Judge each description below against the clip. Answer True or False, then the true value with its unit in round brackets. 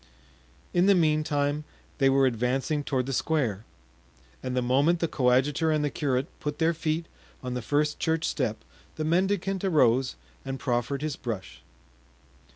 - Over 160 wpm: False (155 wpm)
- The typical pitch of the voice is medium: True (145 Hz)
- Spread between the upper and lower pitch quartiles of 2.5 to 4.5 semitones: True (3.8 semitones)